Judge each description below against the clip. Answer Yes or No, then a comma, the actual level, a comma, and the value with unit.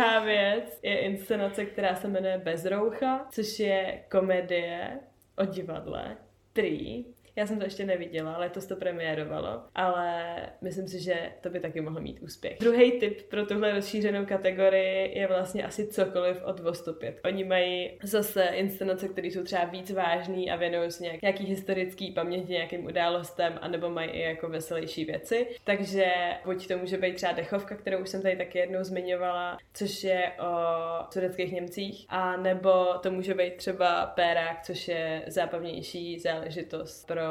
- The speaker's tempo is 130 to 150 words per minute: No, average, 160 wpm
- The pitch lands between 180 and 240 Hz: Yes, medium, 185 Hz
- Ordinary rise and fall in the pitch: No, narrow, 2.0 semitones